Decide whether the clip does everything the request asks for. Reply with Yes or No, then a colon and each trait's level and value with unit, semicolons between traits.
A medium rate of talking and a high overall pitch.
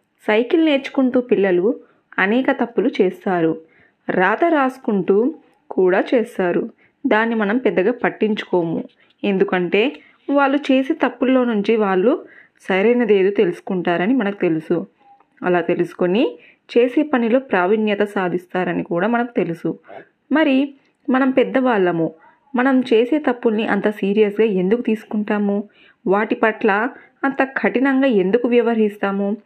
Yes: average, 100 wpm; high, 225 Hz